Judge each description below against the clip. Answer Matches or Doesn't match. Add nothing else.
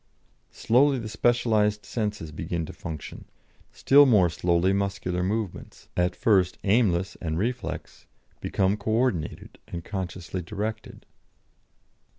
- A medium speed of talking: Doesn't match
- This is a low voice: Matches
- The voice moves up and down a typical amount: Matches